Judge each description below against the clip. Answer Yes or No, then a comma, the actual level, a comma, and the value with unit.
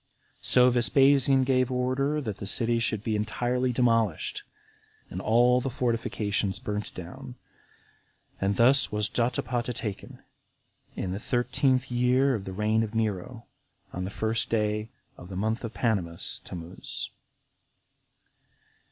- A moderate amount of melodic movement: Yes, average, 3.3 semitones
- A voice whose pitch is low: Yes, low, 115 Hz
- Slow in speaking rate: Yes, slow, 125 wpm